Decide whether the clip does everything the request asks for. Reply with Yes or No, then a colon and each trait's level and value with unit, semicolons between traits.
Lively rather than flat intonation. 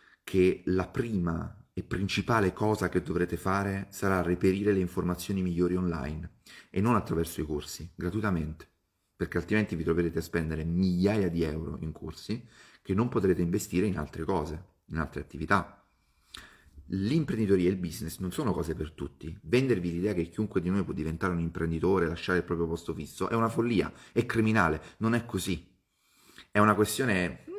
No: average, 3.5 semitones